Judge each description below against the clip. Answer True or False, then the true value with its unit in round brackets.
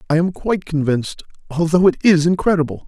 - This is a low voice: False (165 Hz)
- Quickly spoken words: False (165 wpm)